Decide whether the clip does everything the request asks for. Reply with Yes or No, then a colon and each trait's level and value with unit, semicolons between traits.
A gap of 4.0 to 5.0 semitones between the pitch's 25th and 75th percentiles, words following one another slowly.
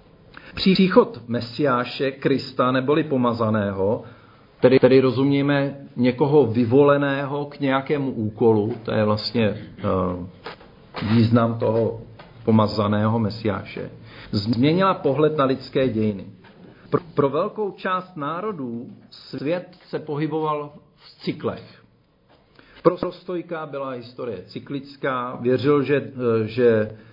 Yes: average, 4.3 semitones; slow, 95 wpm